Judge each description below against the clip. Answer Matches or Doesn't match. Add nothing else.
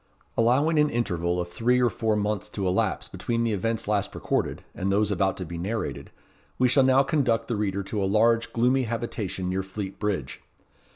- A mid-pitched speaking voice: Doesn't match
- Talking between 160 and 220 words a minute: Matches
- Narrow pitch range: Doesn't match